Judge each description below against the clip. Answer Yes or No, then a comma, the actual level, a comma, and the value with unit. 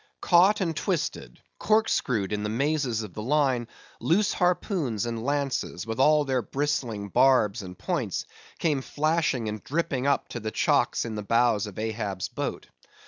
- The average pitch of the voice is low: Yes, low, 125 Hz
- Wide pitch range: Yes, wide, 5.7 semitones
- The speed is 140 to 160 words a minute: Yes, average, 155 wpm